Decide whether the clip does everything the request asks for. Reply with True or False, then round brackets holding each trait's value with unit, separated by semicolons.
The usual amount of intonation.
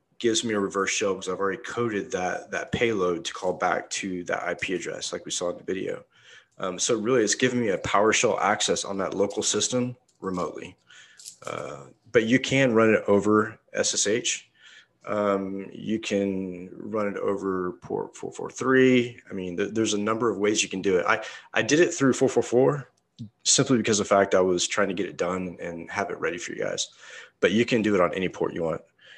True (3.6 semitones)